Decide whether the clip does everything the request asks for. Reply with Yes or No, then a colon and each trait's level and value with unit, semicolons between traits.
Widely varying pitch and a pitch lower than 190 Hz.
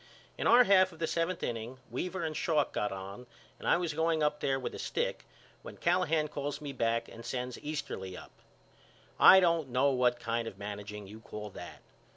Yes: wide, 6.1 semitones; low, 135 Hz